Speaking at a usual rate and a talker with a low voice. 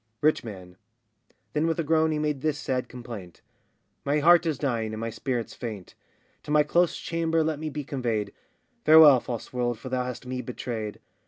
Yes: average, 185 wpm; low, 130 Hz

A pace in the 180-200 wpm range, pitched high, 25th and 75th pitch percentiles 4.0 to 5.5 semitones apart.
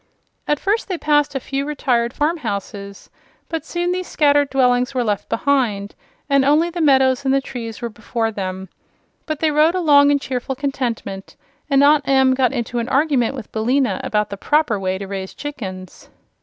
Yes: average, 185 wpm; very high, 265 Hz; average, 4.6 semitones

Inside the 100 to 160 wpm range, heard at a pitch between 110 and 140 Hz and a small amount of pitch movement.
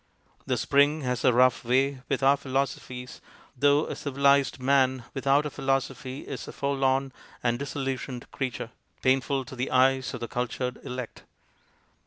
Yes: average, 155 wpm; low, 135 Hz; narrow, 1.5 semitones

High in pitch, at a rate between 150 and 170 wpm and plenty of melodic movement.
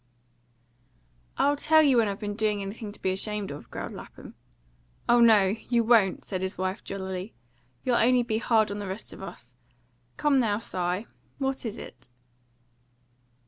No: high, 215 Hz; average, 165 wpm; average, 3.5 semitones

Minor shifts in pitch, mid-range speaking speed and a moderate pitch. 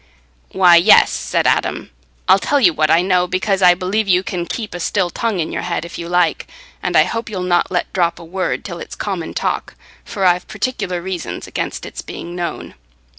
No: narrow, 2.0 semitones; fast, 210 wpm; medium, 180 Hz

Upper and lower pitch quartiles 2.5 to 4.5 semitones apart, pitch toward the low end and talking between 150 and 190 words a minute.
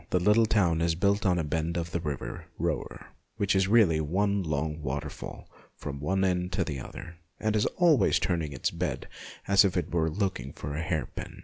No: average, 4.1 semitones; very low, 85 Hz; fast, 205 wpm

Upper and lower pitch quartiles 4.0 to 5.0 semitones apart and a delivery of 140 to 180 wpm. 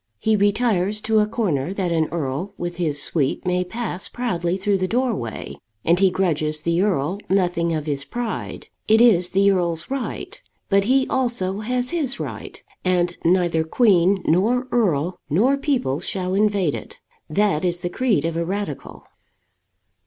Yes: average, 4.4 semitones; average, 160 wpm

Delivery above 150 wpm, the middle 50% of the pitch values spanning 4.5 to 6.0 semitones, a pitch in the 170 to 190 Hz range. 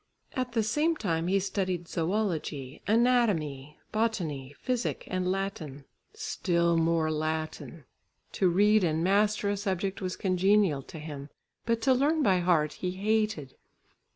No: slow, 135 wpm; average, 5.0 semitones; medium, 185 Hz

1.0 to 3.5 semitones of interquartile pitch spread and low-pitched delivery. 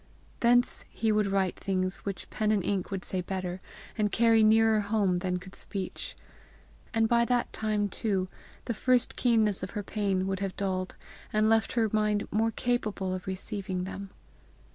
No: average, 2.8 semitones; high, 205 Hz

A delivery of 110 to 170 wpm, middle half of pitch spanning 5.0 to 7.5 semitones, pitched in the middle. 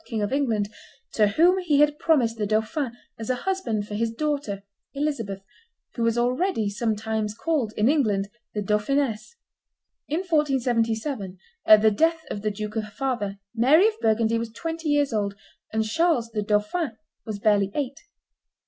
No: average, 160 wpm; wide, 5.6 semitones; high, 230 Hz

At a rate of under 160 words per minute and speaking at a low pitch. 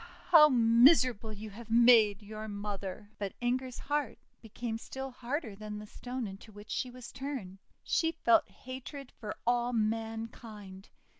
No: average, 145 wpm; high, 230 Hz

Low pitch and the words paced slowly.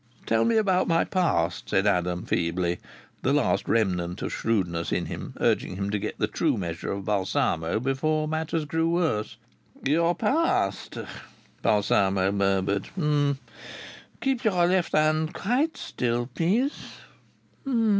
Yes: low, 115 Hz; slow, 130 wpm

